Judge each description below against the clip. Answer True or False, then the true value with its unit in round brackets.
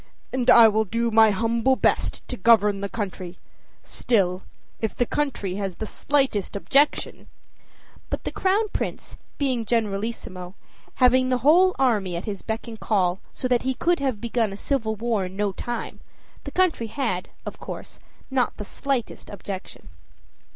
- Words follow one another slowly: False (165 wpm)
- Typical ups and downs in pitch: True (4.2 semitones)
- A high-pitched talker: True (225 Hz)